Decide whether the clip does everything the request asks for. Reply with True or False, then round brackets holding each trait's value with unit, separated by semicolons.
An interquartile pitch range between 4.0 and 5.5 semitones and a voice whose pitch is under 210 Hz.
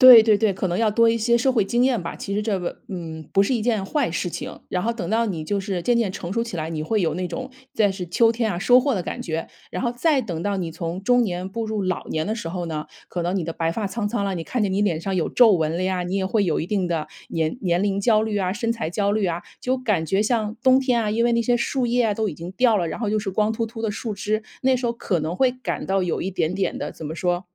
True (4.6 semitones; 200 Hz)